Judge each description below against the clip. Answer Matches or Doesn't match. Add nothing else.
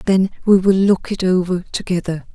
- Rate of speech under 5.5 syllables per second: Matches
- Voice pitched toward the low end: Doesn't match